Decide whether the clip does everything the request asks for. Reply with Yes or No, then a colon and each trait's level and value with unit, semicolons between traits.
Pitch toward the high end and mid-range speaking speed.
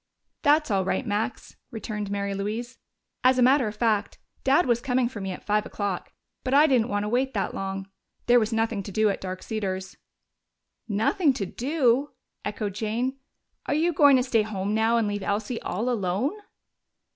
Yes: high, 220 Hz; average, 185 wpm